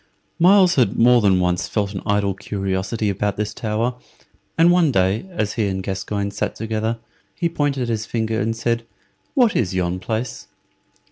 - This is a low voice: Yes, low, 110 Hz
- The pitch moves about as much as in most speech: Yes, average, 3.6 semitones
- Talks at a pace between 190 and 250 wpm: No, average, 165 wpm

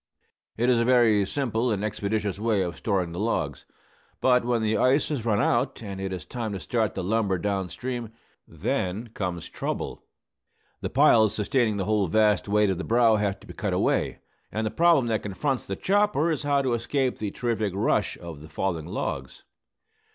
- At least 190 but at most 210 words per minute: Yes, average, 195 wpm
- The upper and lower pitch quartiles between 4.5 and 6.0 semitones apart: No, average, 3.7 semitones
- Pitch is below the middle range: Yes, low, 110 Hz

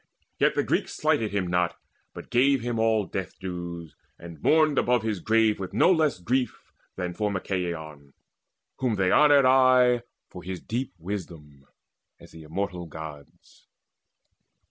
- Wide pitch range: Yes, wide, 6.0 semitones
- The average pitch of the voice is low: Yes, very low, 95 Hz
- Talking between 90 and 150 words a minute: Yes, average, 145 wpm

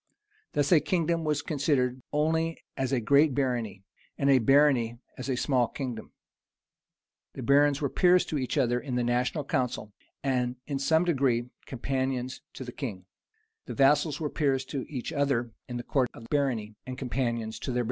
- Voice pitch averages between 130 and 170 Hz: Yes, low, 135 Hz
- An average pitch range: Yes, average, 3.0 semitones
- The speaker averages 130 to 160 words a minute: No, average, 175 wpm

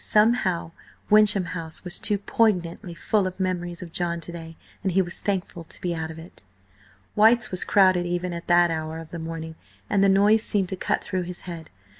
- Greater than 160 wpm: Yes, fast, 205 wpm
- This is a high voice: No, medium, 180 Hz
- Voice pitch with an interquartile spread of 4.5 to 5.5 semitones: No, narrow, 2.6 semitones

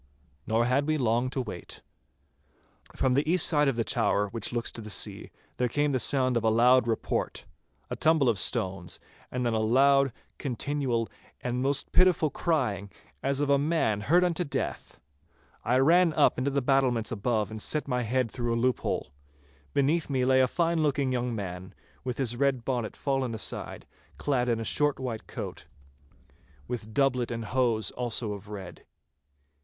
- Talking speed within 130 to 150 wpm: No, average, 175 wpm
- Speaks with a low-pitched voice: Yes, low, 125 Hz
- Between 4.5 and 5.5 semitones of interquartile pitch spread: No, average, 3.5 semitones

